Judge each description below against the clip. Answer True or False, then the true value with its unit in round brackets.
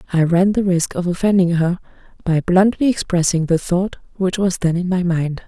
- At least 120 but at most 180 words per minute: False (195 wpm)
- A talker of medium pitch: True (180 Hz)